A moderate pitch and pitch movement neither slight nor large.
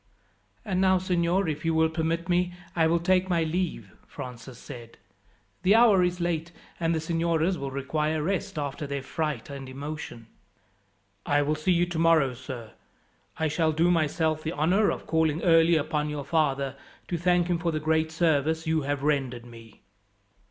Yes: medium, 160 Hz; average, 3.1 semitones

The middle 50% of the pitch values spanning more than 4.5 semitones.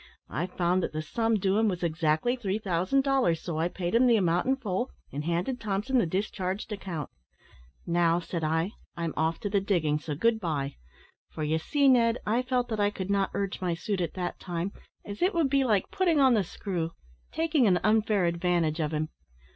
Yes: average, 5.3 semitones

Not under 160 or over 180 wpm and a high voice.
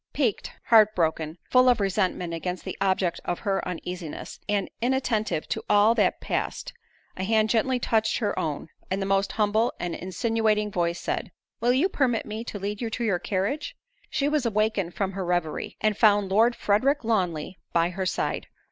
Yes: average, 175 wpm; high, 205 Hz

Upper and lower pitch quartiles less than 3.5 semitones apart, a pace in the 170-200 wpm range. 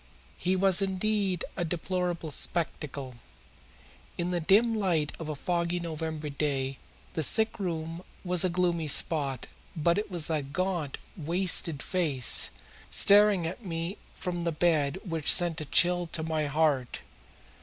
No: average, 2.9 semitones; average, 145 wpm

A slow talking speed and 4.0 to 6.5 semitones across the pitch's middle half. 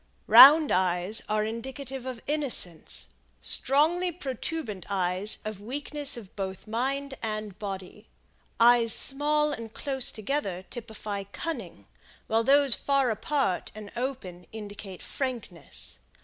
Yes: slow, 115 wpm; wide, 5.5 semitones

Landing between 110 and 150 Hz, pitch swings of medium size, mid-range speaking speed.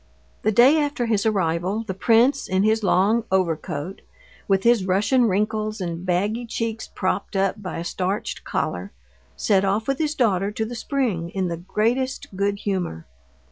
No: high, 205 Hz; average, 3.5 semitones; average, 165 wpm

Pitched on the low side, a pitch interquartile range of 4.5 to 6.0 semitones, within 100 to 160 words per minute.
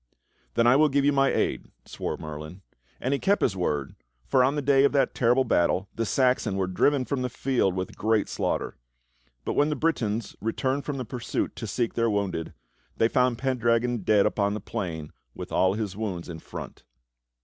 No: low, 115 Hz; average, 5.3 semitones; average, 195 wpm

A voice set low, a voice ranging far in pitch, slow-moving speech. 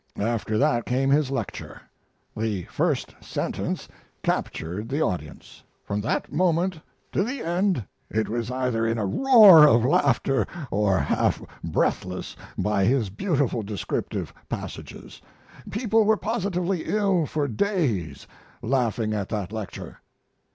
Yes: low, 125 Hz; wide, 8.7 semitones; slow, 125 wpm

